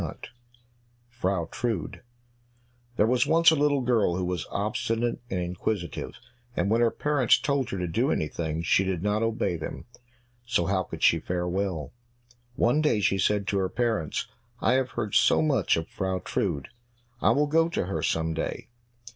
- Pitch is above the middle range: No, low, 100 Hz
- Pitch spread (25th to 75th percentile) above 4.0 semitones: Yes, wide, 5.5 semitones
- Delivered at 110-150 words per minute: No, average, 175 wpm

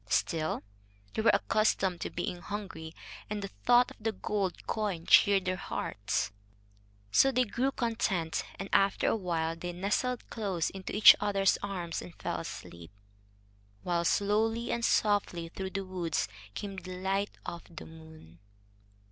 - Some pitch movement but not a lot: Yes, average, 3.6 semitones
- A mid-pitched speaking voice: No, high, 195 Hz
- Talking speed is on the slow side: No, average, 150 wpm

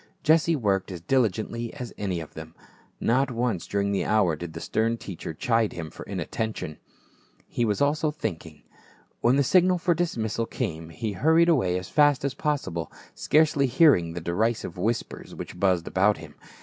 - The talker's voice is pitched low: Yes, low, 110 Hz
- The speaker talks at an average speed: Yes, average, 175 wpm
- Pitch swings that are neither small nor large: No, wide, 7.5 semitones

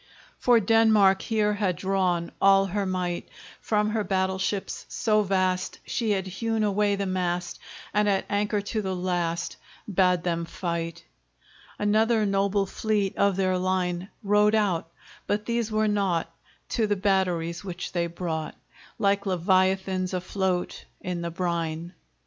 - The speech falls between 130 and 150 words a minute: Yes, average, 145 wpm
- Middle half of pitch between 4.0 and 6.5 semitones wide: No, narrow, 2.5 semitones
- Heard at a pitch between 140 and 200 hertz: Yes, high, 190 Hz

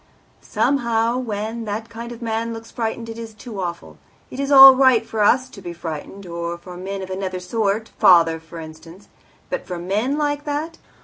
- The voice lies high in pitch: Yes, high, 220 Hz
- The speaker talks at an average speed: Yes, average, 190 wpm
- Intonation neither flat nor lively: Yes, average, 4.5 semitones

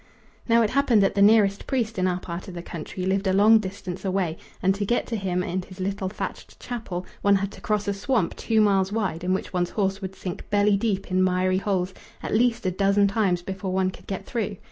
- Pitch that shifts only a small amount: Yes, narrow, 2.1 semitones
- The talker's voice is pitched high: Yes, high, 195 Hz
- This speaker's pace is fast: Yes, fast, 235 wpm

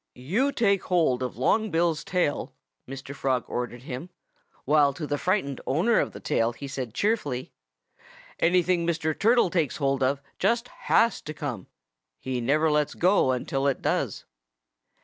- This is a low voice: No, medium, 150 Hz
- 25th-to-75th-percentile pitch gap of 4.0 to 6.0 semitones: Yes, wide, 5.6 semitones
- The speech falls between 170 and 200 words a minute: No, average, 155 wpm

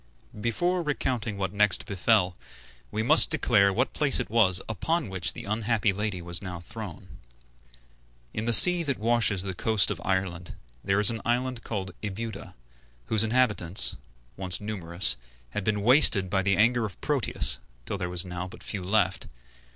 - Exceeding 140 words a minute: Yes, average, 165 wpm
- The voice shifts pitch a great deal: No, average, 3.5 semitones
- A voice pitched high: No, low, 105 Hz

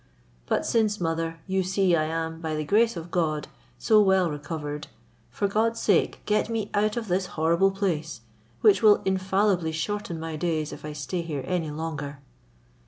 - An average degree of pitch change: Yes, average, 4.1 semitones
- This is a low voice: No, medium, 175 Hz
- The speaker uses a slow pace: No, average, 170 wpm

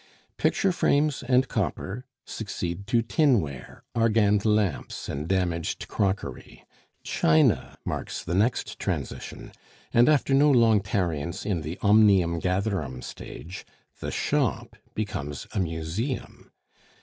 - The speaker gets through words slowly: Yes, slow, 115 wpm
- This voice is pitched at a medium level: No, low, 100 Hz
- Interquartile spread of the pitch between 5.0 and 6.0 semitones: Yes, wide, 5.5 semitones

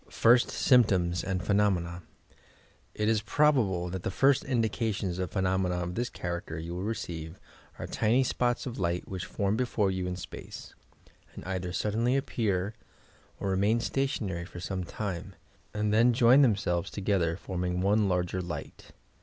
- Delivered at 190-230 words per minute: No, average, 155 wpm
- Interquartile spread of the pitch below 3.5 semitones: No, average, 4.0 semitones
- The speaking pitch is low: Yes, very low, 95 Hz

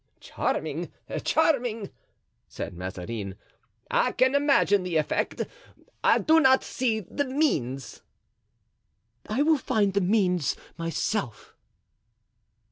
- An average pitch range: No, wide, 8.8 semitones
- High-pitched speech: Yes, high, 205 Hz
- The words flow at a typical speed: No, slow, 100 wpm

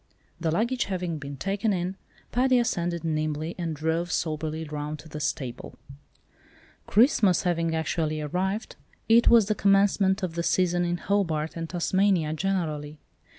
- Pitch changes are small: No, average, 3.8 semitones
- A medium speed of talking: Yes, average, 145 wpm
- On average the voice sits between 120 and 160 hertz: No, medium, 170 Hz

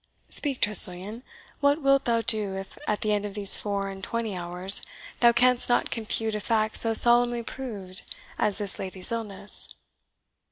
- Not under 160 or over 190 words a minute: Yes, average, 165 wpm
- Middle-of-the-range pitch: No, high, 215 Hz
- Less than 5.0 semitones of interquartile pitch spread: Yes, average, 3.3 semitones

